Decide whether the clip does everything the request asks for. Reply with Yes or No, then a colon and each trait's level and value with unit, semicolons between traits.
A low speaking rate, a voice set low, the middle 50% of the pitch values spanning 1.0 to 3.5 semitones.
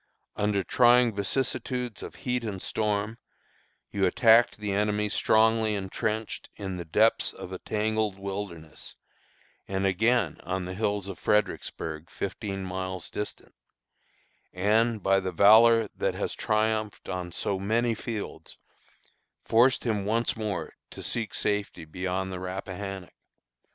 Yes: slow, 130 wpm; low, 105 Hz; average, 2.8 semitones